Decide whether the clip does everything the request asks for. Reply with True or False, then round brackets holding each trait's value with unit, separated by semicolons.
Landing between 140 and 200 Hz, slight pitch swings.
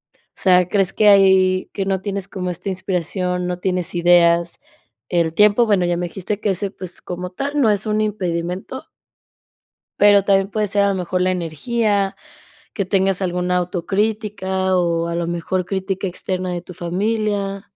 True (190 Hz; 2.1 semitones)